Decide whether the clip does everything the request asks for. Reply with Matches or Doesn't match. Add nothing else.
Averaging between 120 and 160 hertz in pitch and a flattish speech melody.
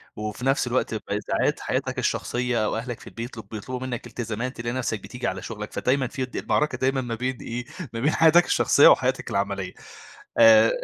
Matches